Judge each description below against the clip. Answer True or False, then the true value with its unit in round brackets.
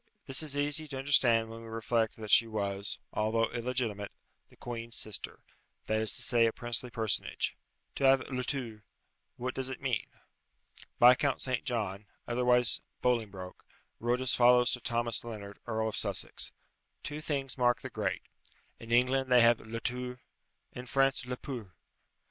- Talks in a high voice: False (120 Hz)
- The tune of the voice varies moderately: False (2.3 semitones)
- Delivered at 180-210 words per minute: False (160 wpm)